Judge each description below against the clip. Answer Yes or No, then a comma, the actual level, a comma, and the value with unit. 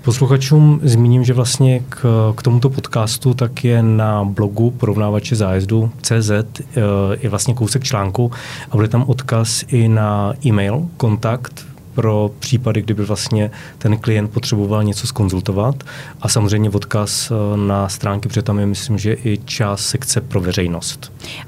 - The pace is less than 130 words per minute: No, average, 140 wpm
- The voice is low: Yes, low, 115 Hz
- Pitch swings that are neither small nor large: Yes, average, 3.5 semitones